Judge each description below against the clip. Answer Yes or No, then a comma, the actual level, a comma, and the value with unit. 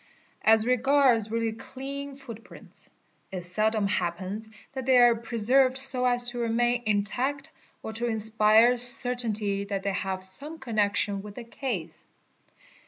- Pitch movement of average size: Yes, average, 3.3 semitones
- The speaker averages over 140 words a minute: No, slow, 135 wpm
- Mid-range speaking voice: No, high, 230 Hz